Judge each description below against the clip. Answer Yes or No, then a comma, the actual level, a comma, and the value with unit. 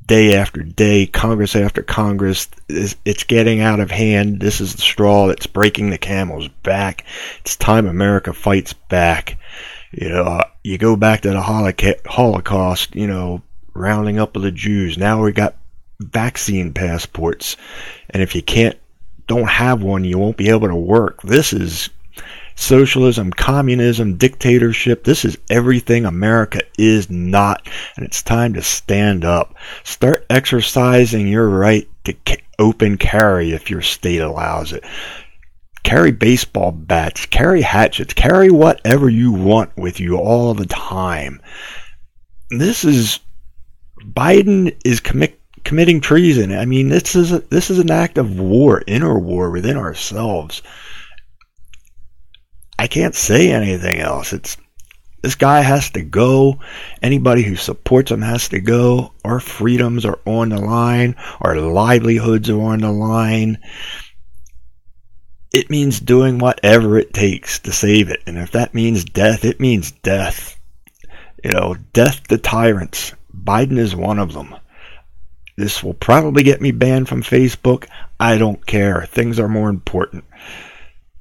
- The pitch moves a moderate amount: Yes, average, 4.1 semitones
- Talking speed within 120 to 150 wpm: Yes, average, 145 wpm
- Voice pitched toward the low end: Yes, low, 105 Hz